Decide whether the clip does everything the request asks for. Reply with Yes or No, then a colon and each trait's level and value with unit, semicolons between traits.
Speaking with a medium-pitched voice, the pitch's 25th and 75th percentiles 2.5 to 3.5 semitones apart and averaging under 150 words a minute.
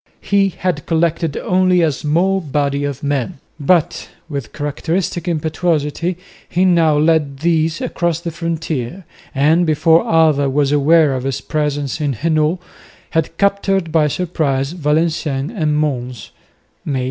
Yes: medium, 155 Hz; average, 2.9 semitones; slow, 135 wpm